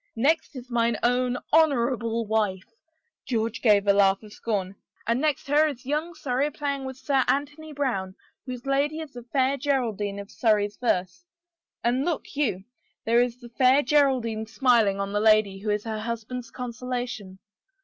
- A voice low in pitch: No, high, 240 Hz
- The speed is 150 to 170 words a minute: Yes, average, 165 wpm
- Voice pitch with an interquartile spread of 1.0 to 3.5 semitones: No, average, 4.1 semitones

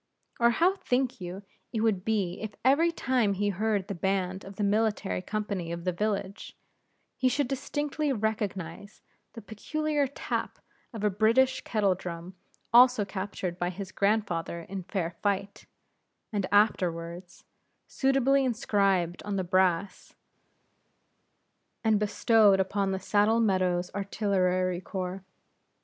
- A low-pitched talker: No, high, 200 Hz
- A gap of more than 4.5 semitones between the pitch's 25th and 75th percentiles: No, average, 3.2 semitones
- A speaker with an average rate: No, slow, 130 wpm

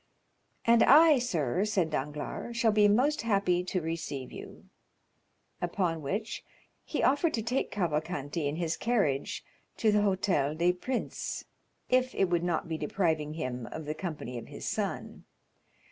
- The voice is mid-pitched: Yes, medium, 175 Hz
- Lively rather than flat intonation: Yes, wide, 5.9 semitones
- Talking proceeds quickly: No, average, 150 wpm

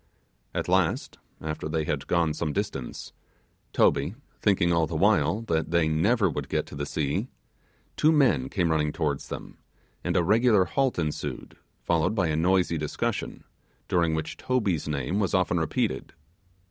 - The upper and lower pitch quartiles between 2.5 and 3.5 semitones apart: No, average, 4.3 semitones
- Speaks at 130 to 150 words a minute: No, average, 160 wpm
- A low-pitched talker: Yes, very low, 85 Hz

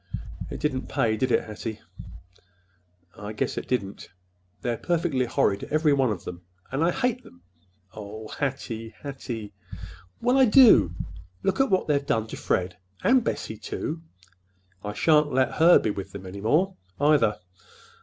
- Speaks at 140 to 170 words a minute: Yes, average, 155 wpm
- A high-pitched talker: No, low, 130 Hz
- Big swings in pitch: Yes, wide, 6.9 semitones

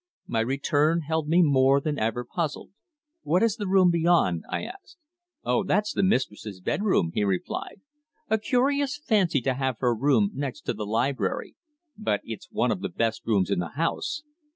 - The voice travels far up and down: Yes, wide, 8.5 semitones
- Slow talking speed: No, average, 175 wpm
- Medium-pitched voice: Yes, medium, 145 Hz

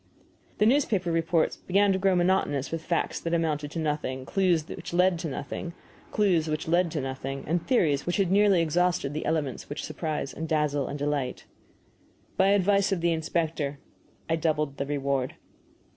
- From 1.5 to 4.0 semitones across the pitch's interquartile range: Yes, average, 3.5 semitones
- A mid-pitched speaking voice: Yes, medium, 165 Hz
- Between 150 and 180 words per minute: Yes, average, 155 wpm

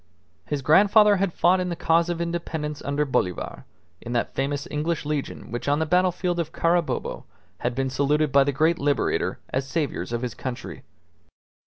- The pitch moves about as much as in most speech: Yes, average, 3.8 semitones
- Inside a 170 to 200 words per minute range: Yes, average, 175 wpm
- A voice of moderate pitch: Yes, medium, 150 Hz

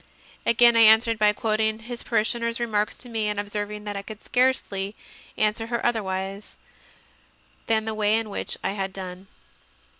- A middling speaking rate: Yes, average, 170 wpm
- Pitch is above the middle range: Yes, high, 215 Hz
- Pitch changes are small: Yes, narrow, 1.9 semitones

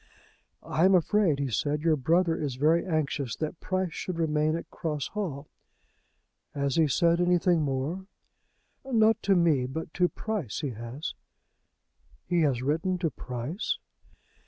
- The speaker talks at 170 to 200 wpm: No, average, 145 wpm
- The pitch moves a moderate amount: Yes, average, 4.0 semitones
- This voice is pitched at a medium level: Yes, medium, 160 Hz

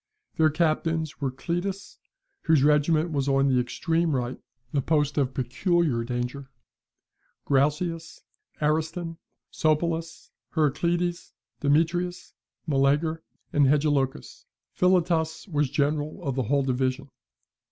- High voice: No, medium, 150 Hz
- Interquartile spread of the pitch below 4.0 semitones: Yes, average, 3.3 semitones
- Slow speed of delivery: Yes, slow, 105 wpm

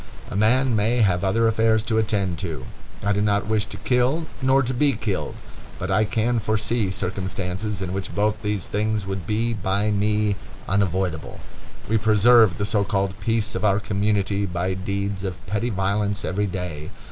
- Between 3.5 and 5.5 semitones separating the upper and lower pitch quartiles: No, narrow, 2.4 semitones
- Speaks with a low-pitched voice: Yes, low, 105 Hz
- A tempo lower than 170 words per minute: No, average, 175 wpm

